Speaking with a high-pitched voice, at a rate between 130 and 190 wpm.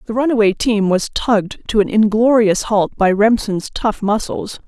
Yes: high, 215 Hz; average, 165 wpm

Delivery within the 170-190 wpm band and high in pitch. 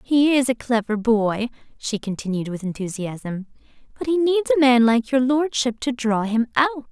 Yes: average, 180 wpm; high, 240 Hz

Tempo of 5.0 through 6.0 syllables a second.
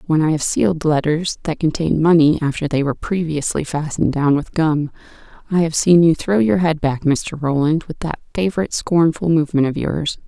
Yes: 5.5 syllables/s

